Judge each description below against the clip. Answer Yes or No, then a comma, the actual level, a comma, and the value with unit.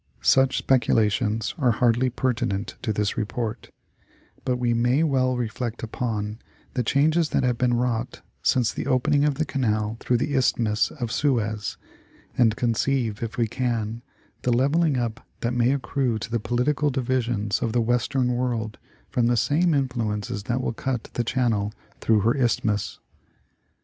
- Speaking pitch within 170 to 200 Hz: No, low, 120 Hz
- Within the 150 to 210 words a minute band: Yes, average, 160 wpm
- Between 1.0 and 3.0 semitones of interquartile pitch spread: Yes, narrow, 2.6 semitones